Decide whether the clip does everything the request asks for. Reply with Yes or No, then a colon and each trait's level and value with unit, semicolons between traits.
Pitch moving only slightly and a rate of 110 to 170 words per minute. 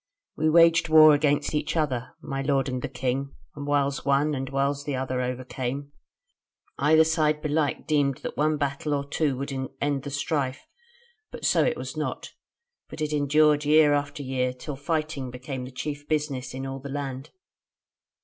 No: narrow, 2.1 semitones; average, 180 wpm